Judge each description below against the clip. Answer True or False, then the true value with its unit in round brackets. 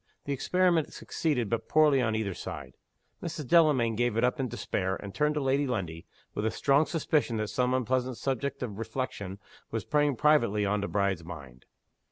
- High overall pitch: False (125 Hz)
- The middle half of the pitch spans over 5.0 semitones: True (5.6 semitones)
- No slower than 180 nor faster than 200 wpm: True (185 wpm)